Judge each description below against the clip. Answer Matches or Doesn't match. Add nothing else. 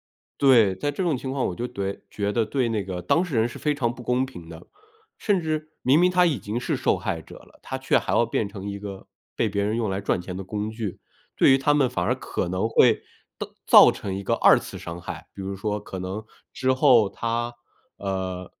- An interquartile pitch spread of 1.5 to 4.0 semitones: Doesn't match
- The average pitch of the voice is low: Matches